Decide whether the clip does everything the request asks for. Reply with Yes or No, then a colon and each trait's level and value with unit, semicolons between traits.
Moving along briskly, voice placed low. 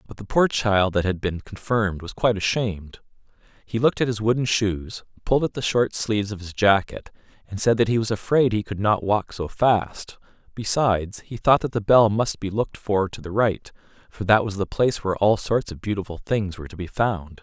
Yes: fast, 225 wpm; low, 105 Hz